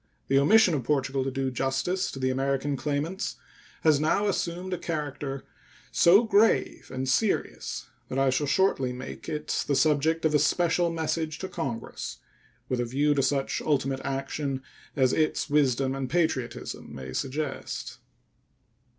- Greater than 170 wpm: No, average, 150 wpm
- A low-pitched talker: No, medium, 145 Hz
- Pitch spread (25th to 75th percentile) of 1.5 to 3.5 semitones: Yes, average, 3.2 semitones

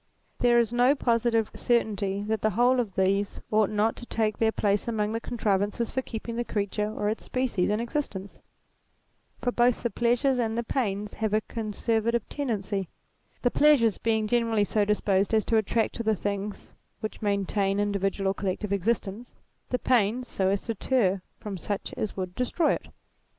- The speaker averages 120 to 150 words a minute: No, average, 175 wpm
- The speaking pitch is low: No, high, 220 Hz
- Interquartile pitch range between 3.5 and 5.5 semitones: No, average, 2.7 semitones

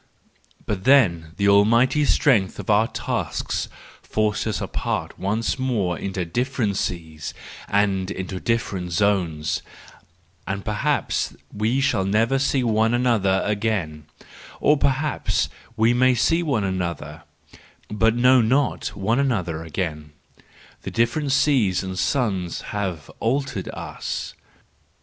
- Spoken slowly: Yes, slow, 115 wpm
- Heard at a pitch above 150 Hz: No, low, 105 Hz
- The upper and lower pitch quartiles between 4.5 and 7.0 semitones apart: Yes, average, 5.1 semitones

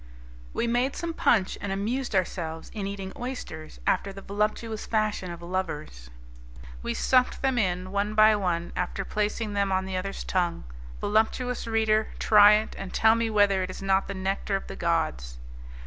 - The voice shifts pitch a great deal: No, average, 2.8 semitones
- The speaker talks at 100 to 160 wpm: No, average, 175 wpm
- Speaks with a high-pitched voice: Yes, high, 200 Hz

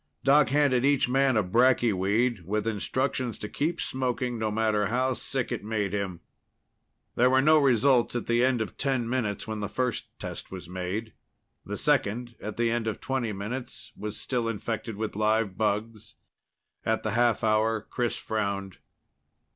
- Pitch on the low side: Yes, low, 115 Hz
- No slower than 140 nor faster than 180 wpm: Yes, average, 170 wpm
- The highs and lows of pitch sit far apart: No, average, 3.2 semitones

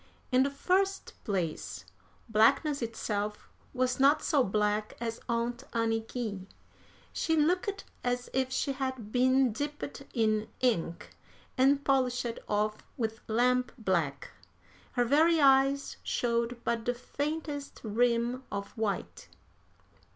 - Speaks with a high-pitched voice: Yes, high, 245 Hz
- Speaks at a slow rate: Yes, slow, 115 wpm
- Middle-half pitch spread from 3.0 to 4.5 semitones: Yes, average, 3.7 semitones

